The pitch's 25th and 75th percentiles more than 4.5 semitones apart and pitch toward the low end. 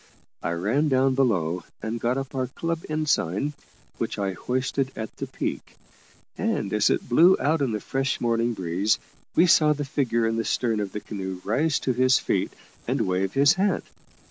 Yes: average, 5.0 semitones; low, 120 Hz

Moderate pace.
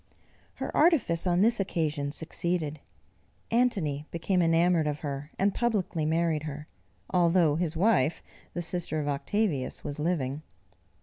No: slow, 130 wpm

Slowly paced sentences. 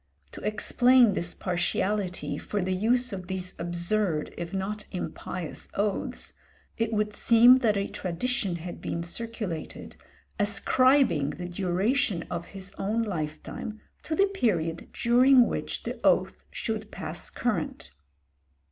Yes: slow, 130 wpm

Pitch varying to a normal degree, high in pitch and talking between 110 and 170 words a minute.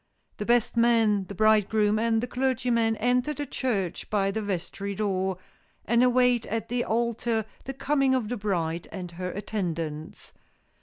Yes: average, 3.6 semitones; high, 220 Hz; average, 155 wpm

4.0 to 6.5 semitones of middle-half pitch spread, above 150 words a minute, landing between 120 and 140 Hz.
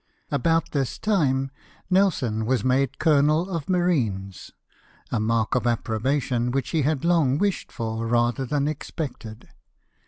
No: average, 4.9 semitones; slow, 135 wpm; low, 135 Hz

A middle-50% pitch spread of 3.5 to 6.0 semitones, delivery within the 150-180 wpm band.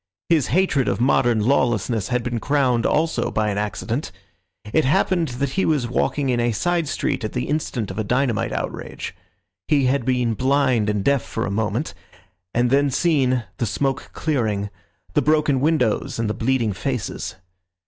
Yes: average, 4.0 semitones; average, 170 wpm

